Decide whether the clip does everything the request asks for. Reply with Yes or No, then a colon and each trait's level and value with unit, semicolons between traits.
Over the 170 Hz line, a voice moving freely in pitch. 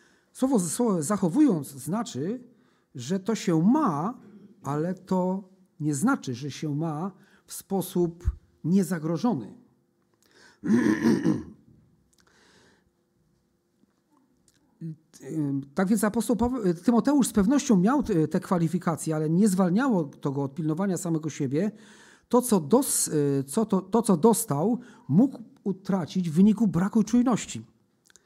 Yes: high, 190 Hz; wide, 6.0 semitones